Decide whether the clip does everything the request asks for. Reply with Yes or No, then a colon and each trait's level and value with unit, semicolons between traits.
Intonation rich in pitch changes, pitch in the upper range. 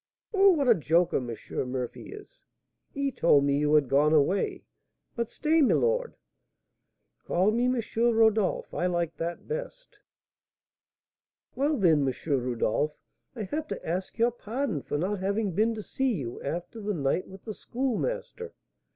Yes: wide, 8.8 semitones; high, 205 Hz